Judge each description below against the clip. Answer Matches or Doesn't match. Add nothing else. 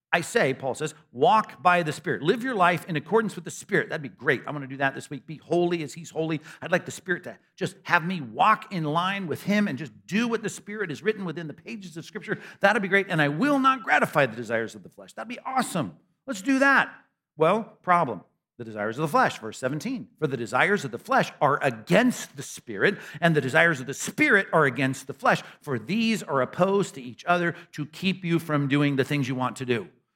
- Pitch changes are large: Matches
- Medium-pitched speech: Matches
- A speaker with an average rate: Doesn't match